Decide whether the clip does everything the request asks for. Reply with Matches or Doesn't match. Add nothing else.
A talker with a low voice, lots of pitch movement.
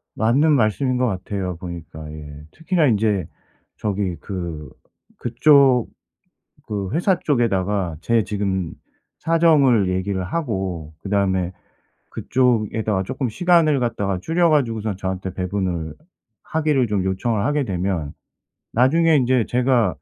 Matches